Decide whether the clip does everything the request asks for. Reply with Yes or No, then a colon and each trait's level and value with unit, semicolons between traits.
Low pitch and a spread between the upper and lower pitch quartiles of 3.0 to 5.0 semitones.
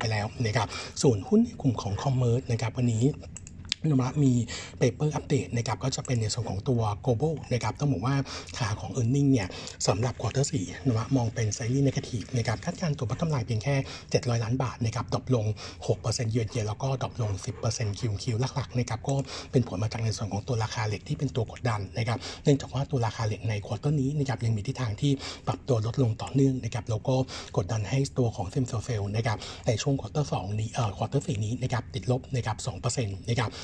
Yes: low, 120 Hz; average, 3.4 semitones